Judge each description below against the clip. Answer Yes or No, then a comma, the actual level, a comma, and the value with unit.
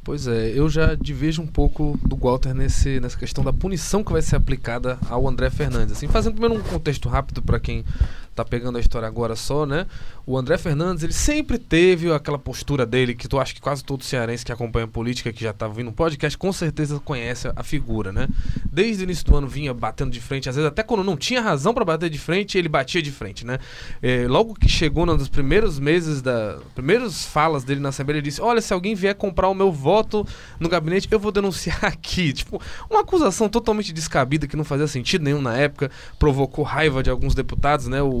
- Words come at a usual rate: No, fast, 220 wpm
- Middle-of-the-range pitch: Yes, medium, 145 Hz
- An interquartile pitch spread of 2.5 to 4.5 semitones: No, average, 5.3 semitones